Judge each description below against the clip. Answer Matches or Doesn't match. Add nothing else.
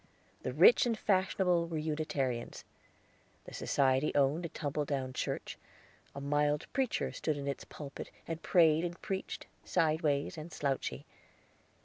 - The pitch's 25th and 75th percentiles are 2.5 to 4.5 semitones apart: Matches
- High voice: Doesn't match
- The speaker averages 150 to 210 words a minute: Doesn't match